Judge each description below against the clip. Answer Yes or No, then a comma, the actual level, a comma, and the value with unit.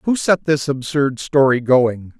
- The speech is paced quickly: No, average, 165 wpm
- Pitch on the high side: No, medium, 140 Hz